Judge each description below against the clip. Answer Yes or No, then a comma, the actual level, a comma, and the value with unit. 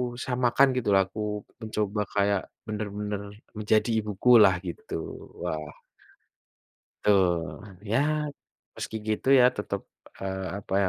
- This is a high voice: No, low, 105 Hz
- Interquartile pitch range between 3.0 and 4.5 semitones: No, narrow, 2.5 semitones